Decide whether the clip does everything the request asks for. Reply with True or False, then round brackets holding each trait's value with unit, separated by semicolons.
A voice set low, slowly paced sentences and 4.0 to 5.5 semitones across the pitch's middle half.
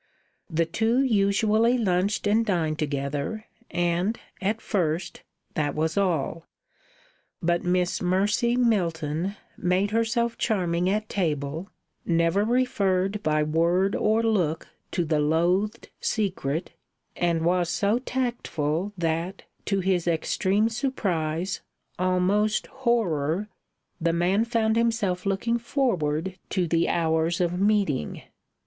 False (185 Hz; 115 wpm; 4.4 semitones)